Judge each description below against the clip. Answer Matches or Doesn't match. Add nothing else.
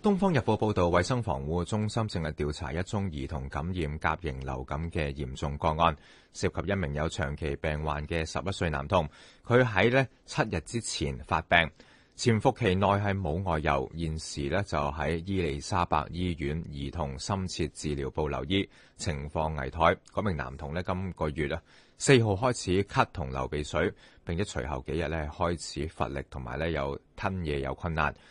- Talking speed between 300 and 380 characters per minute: Doesn't match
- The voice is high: Doesn't match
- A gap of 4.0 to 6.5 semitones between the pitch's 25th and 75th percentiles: Matches